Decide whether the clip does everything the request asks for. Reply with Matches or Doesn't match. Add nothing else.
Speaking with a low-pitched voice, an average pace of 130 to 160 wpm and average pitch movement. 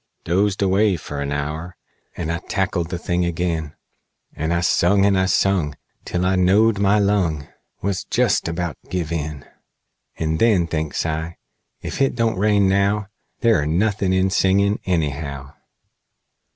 Matches